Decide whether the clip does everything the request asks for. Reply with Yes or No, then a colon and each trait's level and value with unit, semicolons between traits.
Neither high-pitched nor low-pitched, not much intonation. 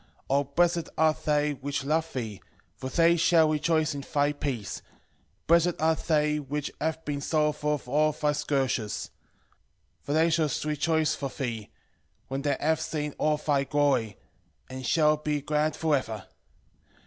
Yes: medium, 150 Hz; narrow, 2.1 semitones